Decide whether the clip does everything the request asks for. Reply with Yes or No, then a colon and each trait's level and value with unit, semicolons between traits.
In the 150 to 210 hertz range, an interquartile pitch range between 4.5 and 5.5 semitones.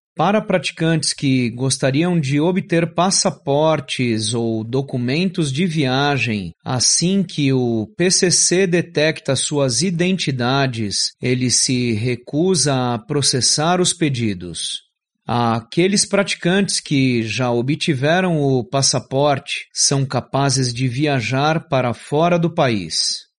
No: medium, 140 Hz; average, 5.2 semitones